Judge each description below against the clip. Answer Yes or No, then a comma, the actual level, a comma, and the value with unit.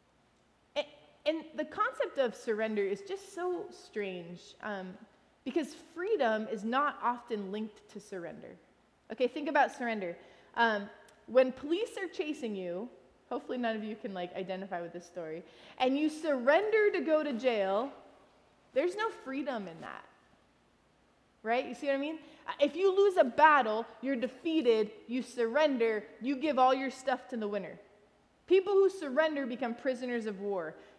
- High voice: Yes, very high, 255 Hz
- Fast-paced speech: No, average, 155 wpm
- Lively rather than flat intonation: Yes, wide, 6.0 semitones